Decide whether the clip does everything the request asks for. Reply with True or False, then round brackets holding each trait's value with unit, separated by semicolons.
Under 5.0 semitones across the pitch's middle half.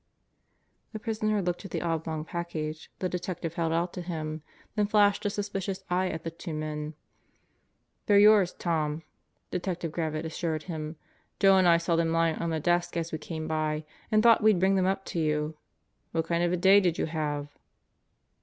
True (3.1 semitones)